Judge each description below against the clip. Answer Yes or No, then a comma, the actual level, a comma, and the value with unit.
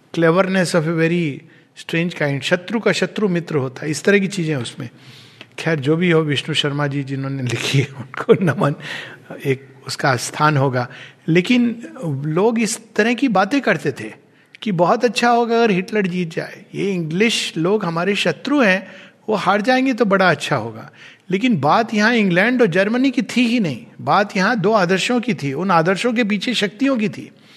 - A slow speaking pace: No, average, 185 wpm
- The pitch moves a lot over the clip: Yes, wide, 6.5 semitones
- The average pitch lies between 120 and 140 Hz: No, medium, 180 Hz